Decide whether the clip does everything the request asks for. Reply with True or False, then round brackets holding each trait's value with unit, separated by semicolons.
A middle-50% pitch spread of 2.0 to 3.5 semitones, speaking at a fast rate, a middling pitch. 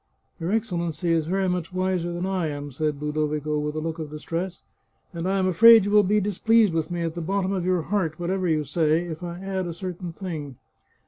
True (3.2 semitones; 245 wpm; 175 Hz)